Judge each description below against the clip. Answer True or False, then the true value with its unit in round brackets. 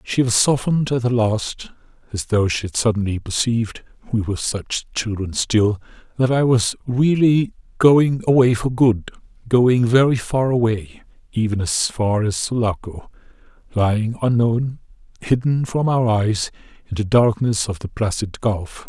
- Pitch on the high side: False (115 Hz)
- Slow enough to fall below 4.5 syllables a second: True (4.2 syllables/s)